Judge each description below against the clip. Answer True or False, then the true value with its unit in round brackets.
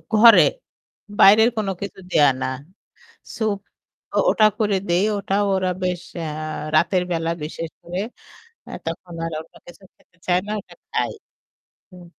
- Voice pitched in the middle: True (180 Hz)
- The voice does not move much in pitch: False (3.2 semitones)